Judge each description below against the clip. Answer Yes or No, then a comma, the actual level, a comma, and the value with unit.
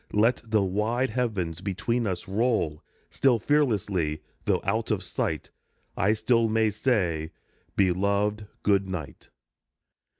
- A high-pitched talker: No, low, 105 Hz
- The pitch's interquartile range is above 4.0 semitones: No, average, 3.7 semitones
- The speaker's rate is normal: No, slow, 125 wpm